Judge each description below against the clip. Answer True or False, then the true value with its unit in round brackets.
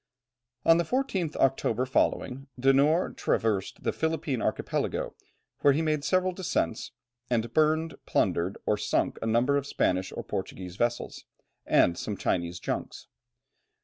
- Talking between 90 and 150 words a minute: True (140 wpm)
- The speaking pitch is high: False (135 Hz)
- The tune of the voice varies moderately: False (6.5 semitones)